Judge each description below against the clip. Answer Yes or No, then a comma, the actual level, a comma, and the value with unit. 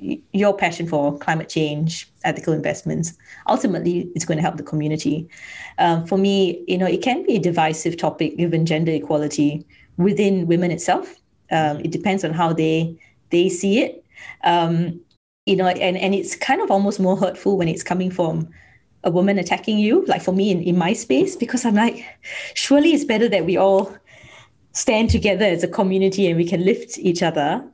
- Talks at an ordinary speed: Yes, average, 185 wpm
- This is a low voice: No, medium, 180 Hz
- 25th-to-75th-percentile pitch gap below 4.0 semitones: Yes, average, 3.2 semitones